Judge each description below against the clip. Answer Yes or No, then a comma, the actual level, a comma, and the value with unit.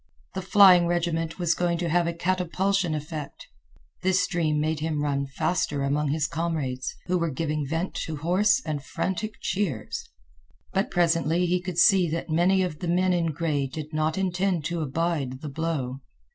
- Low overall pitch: No, medium, 165 Hz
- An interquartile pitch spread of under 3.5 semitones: Yes, average, 2.8 semitones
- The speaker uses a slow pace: No, average, 175 wpm